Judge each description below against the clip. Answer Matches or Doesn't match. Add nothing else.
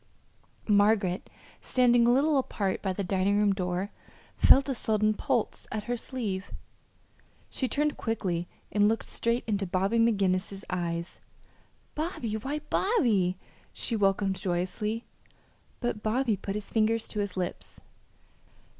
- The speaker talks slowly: Matches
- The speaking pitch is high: Matches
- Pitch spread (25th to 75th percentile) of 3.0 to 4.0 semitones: Matches